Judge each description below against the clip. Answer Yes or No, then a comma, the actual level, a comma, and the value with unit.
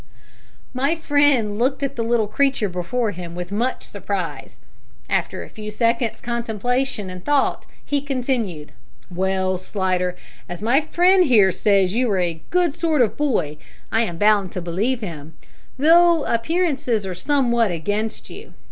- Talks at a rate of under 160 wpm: Yes, average, 150 wpm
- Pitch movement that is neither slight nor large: No, wide, 6.4 semitones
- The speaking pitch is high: Yes, high, 225 Hz